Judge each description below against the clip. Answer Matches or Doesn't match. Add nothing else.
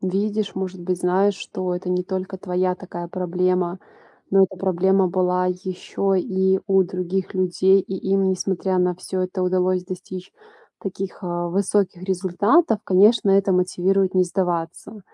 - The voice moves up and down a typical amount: Doesn't match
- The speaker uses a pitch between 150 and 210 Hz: Matches